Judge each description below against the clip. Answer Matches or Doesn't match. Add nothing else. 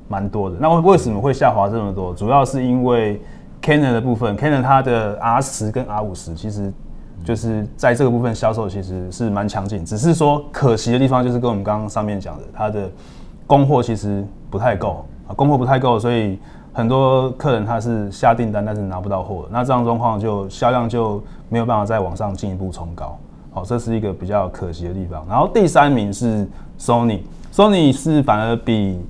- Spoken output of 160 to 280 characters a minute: Doesn't match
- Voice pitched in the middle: Doesn't match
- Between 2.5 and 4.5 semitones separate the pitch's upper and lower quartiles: Matches